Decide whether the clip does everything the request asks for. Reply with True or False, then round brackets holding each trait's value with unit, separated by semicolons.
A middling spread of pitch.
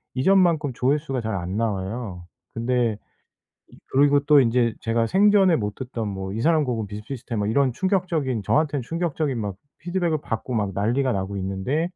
False (6.0 semitones)